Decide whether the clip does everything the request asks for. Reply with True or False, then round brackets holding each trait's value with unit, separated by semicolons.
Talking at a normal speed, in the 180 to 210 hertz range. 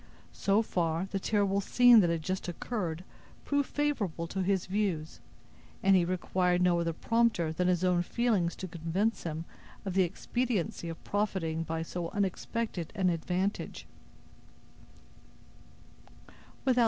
False (130 wpm; 185 Hz)